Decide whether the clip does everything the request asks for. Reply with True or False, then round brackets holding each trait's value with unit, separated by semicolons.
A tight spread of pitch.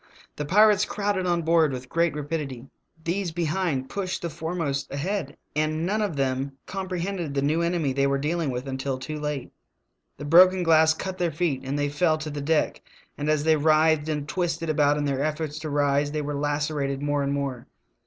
False (3.1 semitones)